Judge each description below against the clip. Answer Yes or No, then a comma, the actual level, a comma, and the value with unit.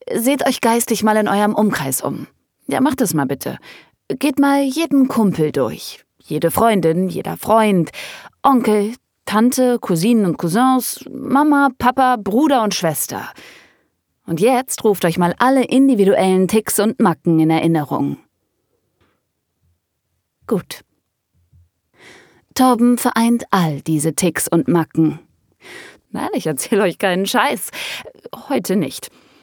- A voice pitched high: Yes, high, 210 Hz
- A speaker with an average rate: No, slow, 120 wpm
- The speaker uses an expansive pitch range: Yes, wide, 7.0 semitones